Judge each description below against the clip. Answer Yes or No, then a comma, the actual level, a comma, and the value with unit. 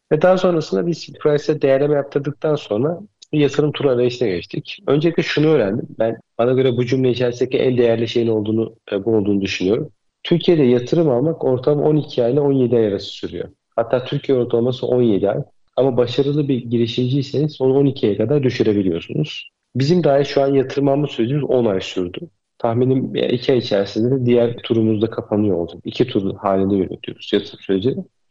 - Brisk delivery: Yes, fast, 165 wpm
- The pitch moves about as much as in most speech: Yes, average, 4.2 semitones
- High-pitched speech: No, low, 130 Hz